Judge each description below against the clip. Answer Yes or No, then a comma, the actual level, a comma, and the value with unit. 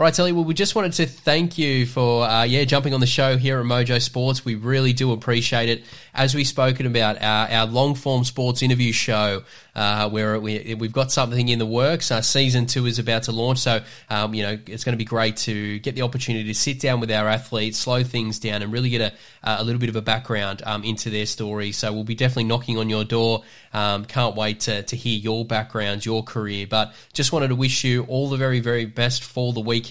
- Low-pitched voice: Yes, low, 120 Hz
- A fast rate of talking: Yes, fast, 240 wpm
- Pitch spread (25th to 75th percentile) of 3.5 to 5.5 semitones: No, average, 2.9 semitones